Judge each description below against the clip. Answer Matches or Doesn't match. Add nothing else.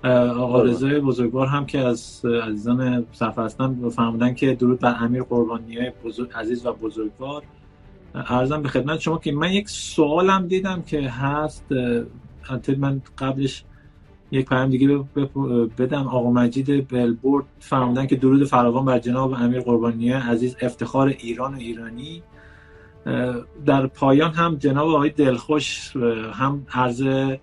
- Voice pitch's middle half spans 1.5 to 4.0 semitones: Matches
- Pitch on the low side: Matches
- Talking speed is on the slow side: Doesn't match